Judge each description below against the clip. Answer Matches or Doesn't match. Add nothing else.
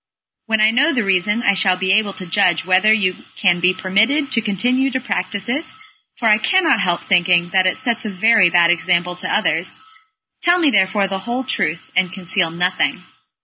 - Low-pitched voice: Doesn't match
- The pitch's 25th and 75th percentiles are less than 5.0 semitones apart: Matches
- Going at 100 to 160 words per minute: Doesn't match